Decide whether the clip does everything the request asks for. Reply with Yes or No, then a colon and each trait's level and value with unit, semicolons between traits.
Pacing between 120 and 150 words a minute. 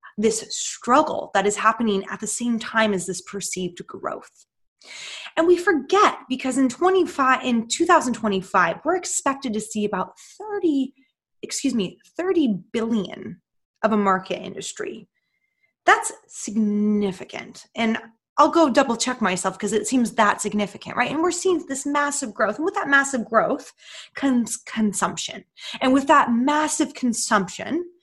Yes: average, 145 wpm